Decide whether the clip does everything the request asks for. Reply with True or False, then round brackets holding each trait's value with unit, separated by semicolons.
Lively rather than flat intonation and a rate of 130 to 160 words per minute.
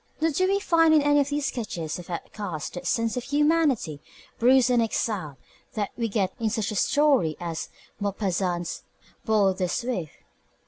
False (7.6 semitones; 170 wpm)